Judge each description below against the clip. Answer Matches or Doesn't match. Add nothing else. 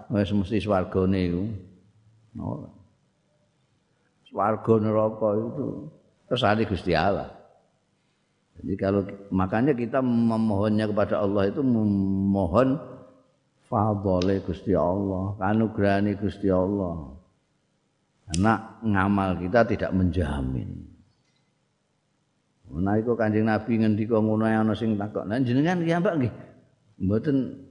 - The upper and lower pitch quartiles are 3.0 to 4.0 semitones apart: Doesn't match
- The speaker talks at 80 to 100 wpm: Matches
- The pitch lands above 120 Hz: Doesn't match